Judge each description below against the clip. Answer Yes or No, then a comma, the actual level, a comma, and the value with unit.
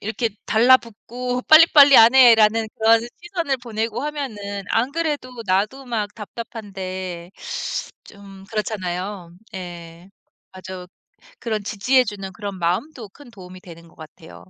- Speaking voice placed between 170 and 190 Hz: No, high, 215 Hz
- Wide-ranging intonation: No, average, 4.8 semitones